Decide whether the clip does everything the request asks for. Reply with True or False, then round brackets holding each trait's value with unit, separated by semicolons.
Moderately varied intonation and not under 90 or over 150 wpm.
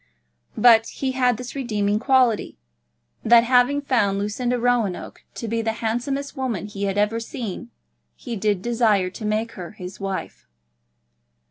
True (3.1 semitones; 145 wpm)